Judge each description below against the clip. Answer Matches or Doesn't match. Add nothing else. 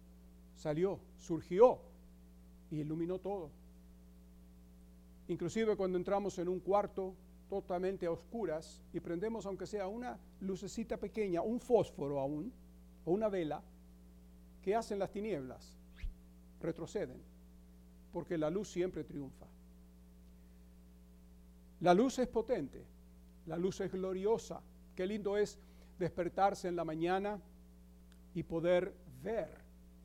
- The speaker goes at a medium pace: Doesn't match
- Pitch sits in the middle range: Matches